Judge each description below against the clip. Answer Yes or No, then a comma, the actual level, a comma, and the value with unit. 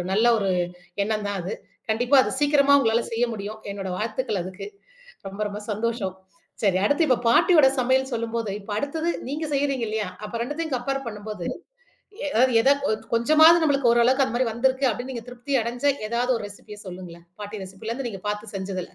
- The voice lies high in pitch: Yes, high, 230 Hz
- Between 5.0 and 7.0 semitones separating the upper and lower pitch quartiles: No, average, 4.2 semitones